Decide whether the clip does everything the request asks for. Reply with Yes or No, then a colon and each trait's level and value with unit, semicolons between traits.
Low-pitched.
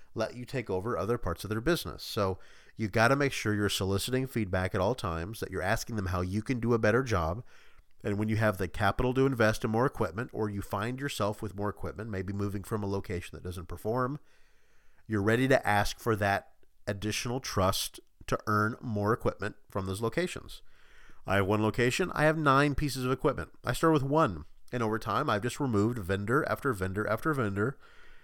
Yes: low, 110 Hz